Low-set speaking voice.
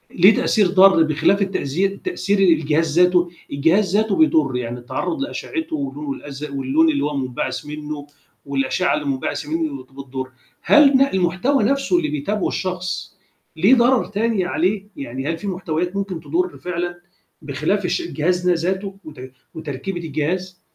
No: medium, 175 Hz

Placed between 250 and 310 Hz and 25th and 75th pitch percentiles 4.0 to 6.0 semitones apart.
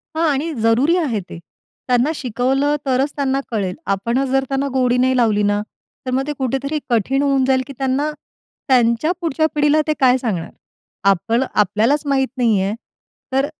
No: very high, 260 Hz; average, 3.2 semitones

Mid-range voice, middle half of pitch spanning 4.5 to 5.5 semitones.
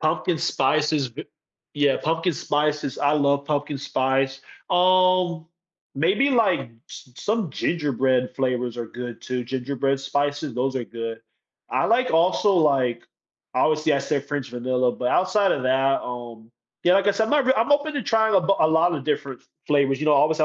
Yes: medium, 145 Hz; average, 5.0 semitones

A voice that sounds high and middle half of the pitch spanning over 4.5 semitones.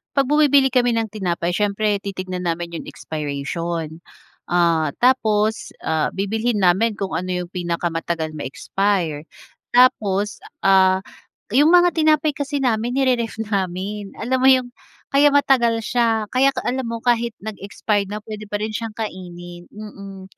Yes: high, 210 Hz; average, 5.2 semitones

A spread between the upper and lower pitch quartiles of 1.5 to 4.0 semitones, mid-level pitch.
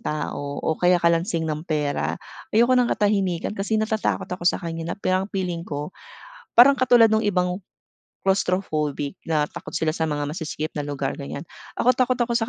No: wide, 5.6 semitones; medium, 180 Hz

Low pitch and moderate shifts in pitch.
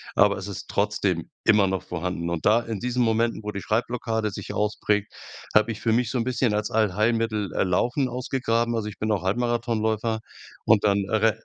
No: low, 110 Hz; narrow, 2.3 semitones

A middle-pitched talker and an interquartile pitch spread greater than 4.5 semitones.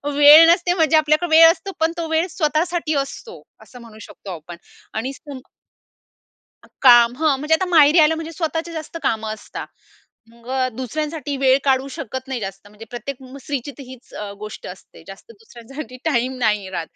No: very high, 275 Hz; average, 5.0 semitones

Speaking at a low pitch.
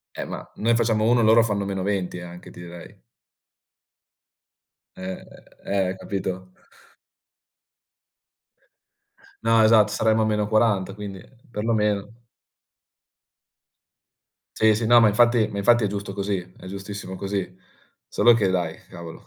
Yes: low, 100 Hz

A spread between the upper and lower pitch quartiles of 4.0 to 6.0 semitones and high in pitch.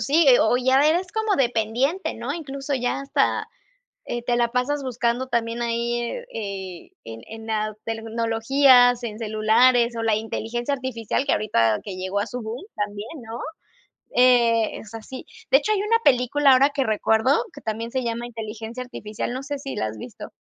No: average, 3.3 semitones; high, 240 Hz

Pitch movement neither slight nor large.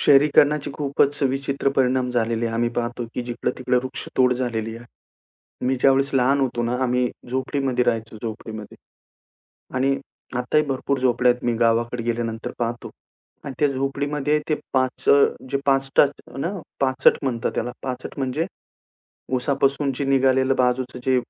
No: narrow, 2.2 semitones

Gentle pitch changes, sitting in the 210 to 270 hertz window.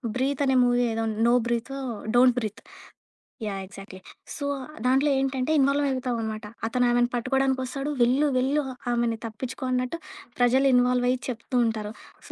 Yes: narrow, 2.2 semitones; very high, 250 Hz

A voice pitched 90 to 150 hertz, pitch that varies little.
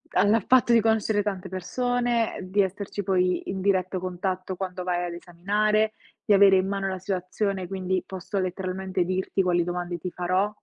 No: high, 190 Hz; narrow, 1.9 semitones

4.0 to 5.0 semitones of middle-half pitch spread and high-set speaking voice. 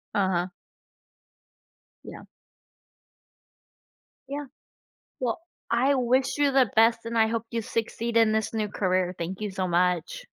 Yes: average, 4.7 semitones; high, 225 Hz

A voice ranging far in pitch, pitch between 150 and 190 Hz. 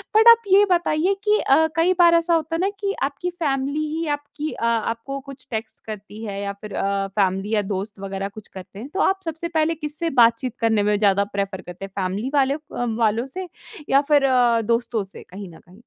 No: wide, 8.0 semitones; high, 235 Hz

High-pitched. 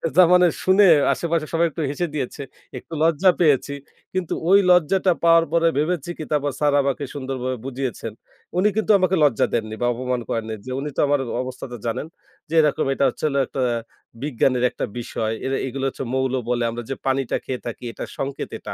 No: medium, 140 Hz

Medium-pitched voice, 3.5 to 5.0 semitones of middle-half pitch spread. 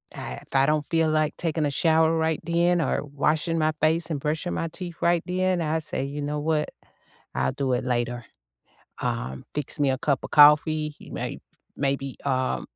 No: medium, 150 Hz; average, 2.7 semitones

